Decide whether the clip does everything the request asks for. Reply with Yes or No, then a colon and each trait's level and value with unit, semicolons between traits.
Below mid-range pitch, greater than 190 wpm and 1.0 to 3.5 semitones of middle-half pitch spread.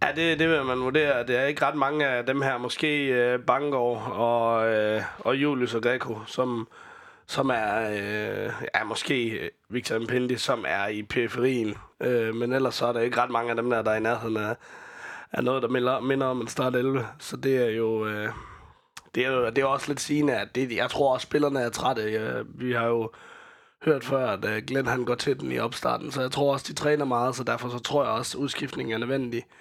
Yes: low, 125 Hz; fast, 225 wpm; average, 2.7 semitones